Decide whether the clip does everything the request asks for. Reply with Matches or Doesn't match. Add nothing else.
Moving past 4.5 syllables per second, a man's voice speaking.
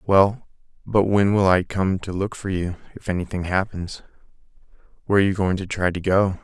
Matches